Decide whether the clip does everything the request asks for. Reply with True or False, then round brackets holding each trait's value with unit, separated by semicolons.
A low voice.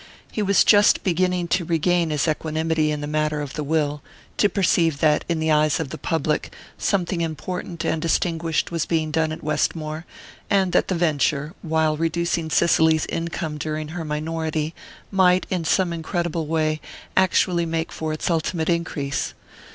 False (160 Hz)